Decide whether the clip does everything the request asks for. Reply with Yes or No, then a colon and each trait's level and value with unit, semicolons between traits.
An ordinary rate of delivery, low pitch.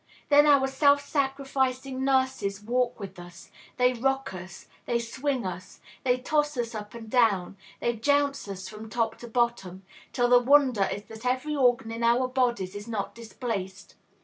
No: average, 170 wpm; high, 240 Hz